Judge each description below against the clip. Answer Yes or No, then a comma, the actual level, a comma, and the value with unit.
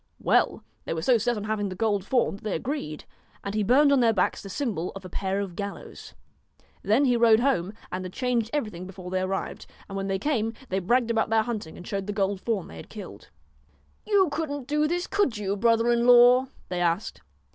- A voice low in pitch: No, high, 215 Hz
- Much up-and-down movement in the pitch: No, average, 4.3 semitones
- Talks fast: Yes, fast, 230 wpm